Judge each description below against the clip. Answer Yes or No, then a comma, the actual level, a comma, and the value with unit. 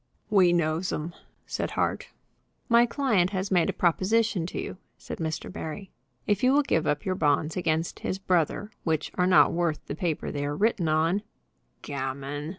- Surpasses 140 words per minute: Yes, average, 180 wpm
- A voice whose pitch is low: No, medium, 175 Hz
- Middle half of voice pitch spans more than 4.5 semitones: No, average, 3.8 semitones